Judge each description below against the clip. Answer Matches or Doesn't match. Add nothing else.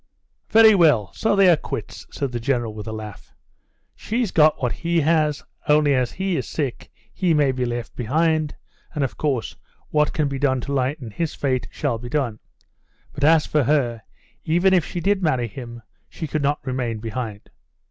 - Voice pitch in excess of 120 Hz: Matches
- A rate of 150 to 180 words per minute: Doesn't match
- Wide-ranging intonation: Doesn't match